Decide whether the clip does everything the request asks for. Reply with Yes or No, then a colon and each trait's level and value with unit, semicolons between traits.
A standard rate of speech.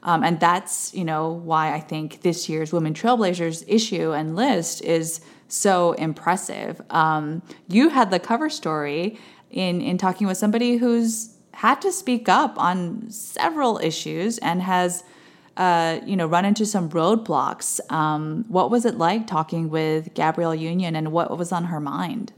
Yes: average, 165 wpm